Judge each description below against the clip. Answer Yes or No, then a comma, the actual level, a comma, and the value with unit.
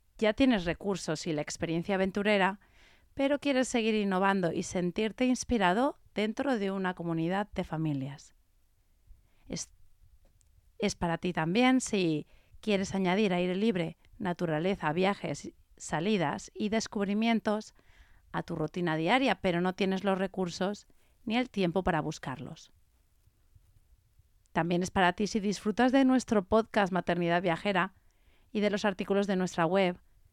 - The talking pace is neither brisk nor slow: Yes, average, 135 wpm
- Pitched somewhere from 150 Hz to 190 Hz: Yes, medium, 185 Hz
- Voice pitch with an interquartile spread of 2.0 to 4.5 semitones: No, average, 5.0 semitones